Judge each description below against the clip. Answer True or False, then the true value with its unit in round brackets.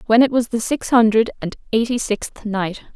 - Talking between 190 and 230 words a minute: True (205 wpm)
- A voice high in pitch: True (225 Hz)